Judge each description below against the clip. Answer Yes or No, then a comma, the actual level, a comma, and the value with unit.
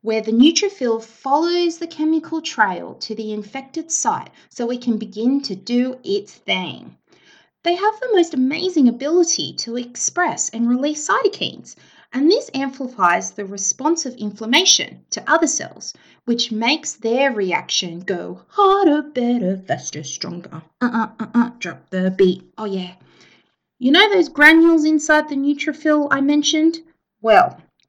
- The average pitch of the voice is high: Yes, very high, 270 Hz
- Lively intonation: Yes, wide, 6.4 semitones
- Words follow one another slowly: No, average, 150 wpm